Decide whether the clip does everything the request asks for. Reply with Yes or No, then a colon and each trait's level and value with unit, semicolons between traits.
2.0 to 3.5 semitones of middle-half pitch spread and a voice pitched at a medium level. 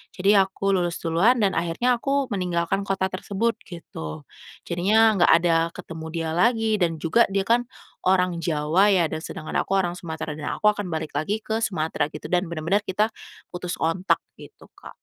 Yes: average, 3.1 semitones; medium, 180 Hz